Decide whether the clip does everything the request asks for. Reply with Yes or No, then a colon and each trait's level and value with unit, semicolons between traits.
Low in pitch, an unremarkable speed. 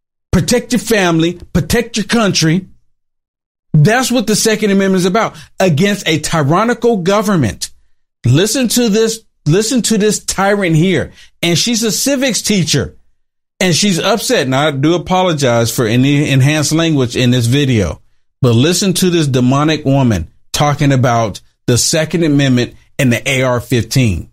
No: medium, 160 Hz; average, 145 wpm